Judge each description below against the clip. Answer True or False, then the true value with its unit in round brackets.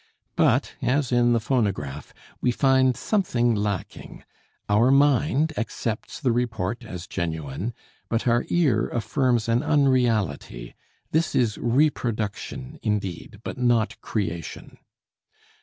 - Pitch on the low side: True (120 Hz)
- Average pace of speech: False (110 wpm)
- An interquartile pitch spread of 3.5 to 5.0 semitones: True (3.9 semitones)